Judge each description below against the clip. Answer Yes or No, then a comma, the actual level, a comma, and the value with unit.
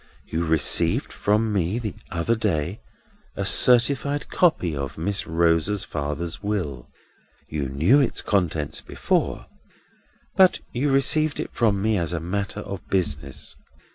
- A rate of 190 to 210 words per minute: No, slow, 135 wpm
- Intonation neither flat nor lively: No, wide, 5.9 semitones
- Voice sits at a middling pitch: No, very low, 95 Hz